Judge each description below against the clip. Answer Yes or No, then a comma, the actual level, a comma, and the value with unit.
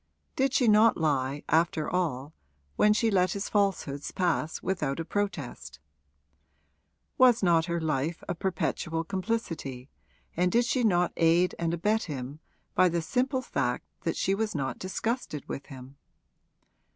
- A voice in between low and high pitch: Yes, medium, 170 Hz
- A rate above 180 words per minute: No, average, 145 wpm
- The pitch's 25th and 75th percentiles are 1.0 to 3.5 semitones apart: No, average, 5.2 semitones